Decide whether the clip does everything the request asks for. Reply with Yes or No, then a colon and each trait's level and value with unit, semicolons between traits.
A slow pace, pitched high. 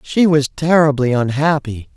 No: slow, 120 wpm; medium, 145 Hz